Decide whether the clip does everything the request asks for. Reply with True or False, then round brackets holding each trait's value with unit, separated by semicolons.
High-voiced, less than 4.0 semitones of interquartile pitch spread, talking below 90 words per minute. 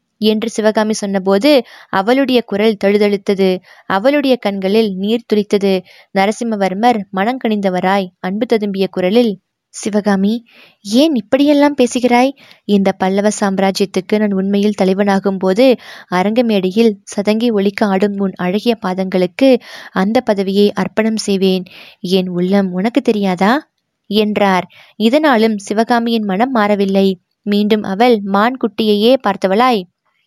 False (205 Hz; 3.1 semitones; 105 wpm)